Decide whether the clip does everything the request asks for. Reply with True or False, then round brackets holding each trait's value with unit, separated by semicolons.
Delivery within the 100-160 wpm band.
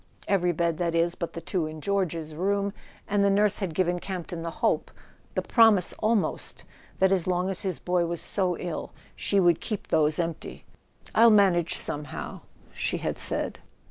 False (180 wpm)